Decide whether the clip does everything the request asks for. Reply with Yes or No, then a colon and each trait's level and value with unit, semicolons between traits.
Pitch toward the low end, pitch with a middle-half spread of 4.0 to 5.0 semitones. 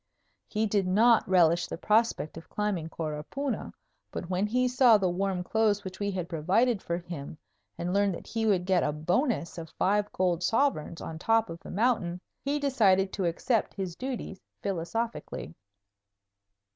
No: high, 195 Hz; average, 4.5 semitones